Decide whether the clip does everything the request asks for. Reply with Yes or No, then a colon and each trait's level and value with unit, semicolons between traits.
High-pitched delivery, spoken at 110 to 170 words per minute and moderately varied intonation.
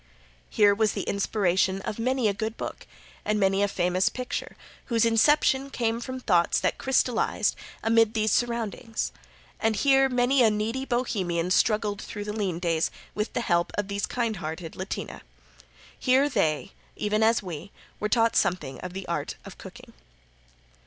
Yes: high, 215 Hz; average, 160 wpm; average, 3.6 semitones